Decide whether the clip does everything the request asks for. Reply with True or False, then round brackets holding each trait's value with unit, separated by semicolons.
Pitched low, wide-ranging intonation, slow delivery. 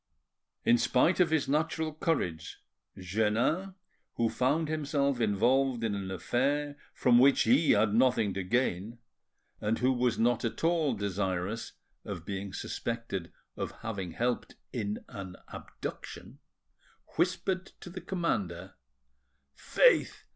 True (120 Hz; 6.2 semitones; 125 wpm)